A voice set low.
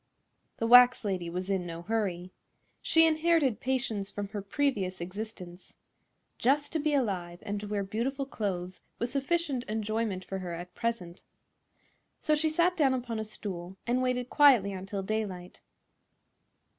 No: high, 215 Hz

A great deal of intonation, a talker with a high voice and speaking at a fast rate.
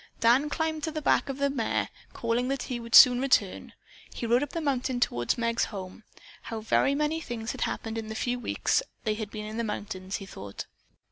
No: average, 3.9 semitones; high, 235 Hz; fast, 215 wpm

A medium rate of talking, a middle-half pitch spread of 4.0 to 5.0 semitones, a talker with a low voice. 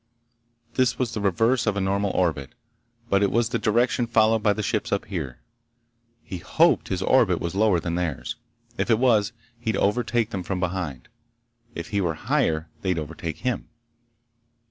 Yes: average, 170 wpm; average, 4.5 semitones; low, 100 Hz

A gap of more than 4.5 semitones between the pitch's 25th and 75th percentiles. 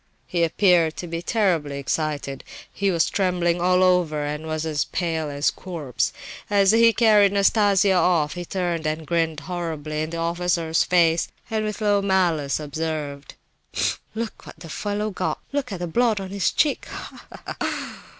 No: average, 3.8 semitones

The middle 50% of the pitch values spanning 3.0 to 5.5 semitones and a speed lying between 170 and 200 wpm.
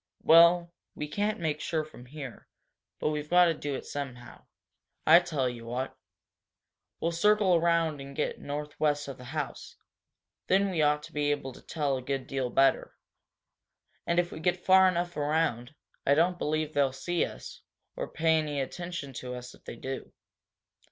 Yes: average, 3.8 semitones; average, 175 wpm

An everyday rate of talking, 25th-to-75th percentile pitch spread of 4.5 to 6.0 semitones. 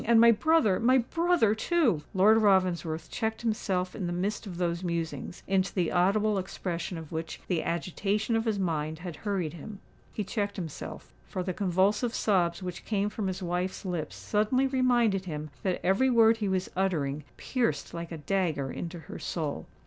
No: average, 170 wpm; average, 4.1 semitones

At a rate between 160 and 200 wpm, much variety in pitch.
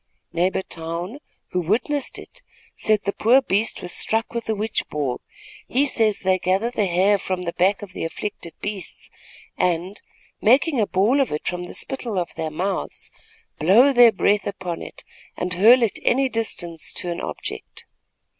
No: average, 175 wpm; average, 4.4 semitones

